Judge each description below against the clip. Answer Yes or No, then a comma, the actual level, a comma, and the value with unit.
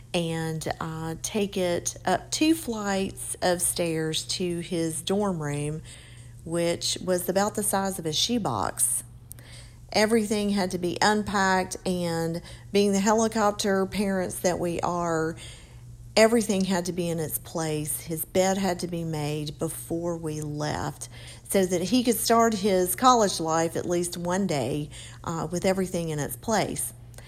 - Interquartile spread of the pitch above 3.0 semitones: Yes, average, 4.4 semitones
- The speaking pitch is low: No, medium, 175 Hz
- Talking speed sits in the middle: Yes, average, 150 wpm